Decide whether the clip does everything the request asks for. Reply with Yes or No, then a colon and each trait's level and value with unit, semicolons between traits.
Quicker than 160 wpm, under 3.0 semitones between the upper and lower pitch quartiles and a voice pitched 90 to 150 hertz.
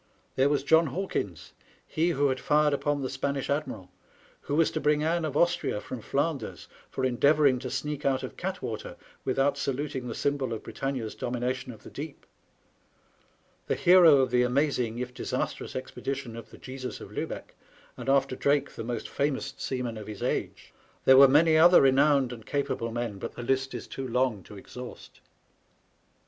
Yes: average, 175 wpm; narrow, 2.6 semitones; low, 135 Hz